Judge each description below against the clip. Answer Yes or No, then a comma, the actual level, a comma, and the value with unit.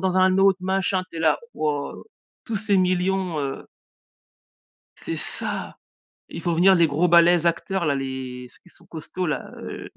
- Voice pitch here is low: No, medium, 175 Hz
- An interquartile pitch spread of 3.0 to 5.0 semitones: Yes, average, 3.6 semitones